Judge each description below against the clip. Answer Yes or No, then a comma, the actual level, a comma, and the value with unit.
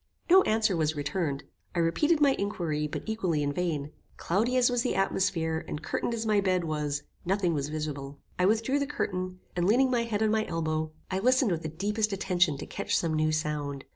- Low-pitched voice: No, medium, 180 Hz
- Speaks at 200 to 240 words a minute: Yes, fast, 205 wpm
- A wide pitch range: Yes, wide, 5.8 semitones